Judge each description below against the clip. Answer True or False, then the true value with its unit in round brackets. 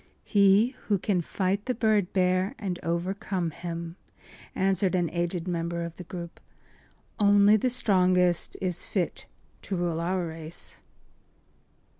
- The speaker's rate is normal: False (130 wpm)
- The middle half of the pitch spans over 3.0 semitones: False (2.6 semitones)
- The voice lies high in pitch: False (180 Hz)